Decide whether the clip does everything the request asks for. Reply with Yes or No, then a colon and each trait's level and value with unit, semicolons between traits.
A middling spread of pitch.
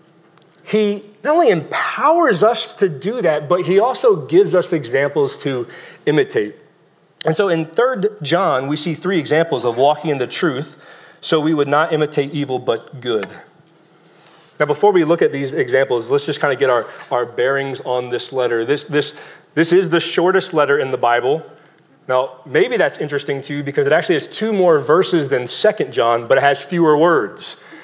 No: wide, 6.7 semitones